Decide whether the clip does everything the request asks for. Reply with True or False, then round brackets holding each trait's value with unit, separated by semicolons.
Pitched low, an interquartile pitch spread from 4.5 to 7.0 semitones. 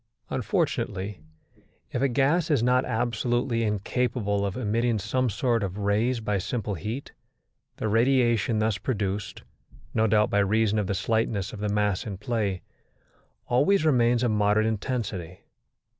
False (110 Hz; 3.1 semitones)